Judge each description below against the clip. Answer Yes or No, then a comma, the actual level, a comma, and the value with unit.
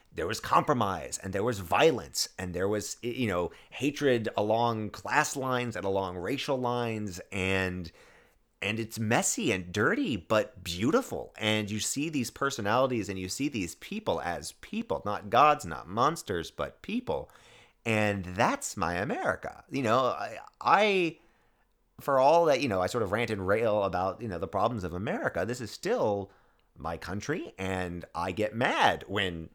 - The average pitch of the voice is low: Yes, low, 110 Hz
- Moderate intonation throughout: Yes, average, 5.0 semitones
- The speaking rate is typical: Yes, average, 165 wpm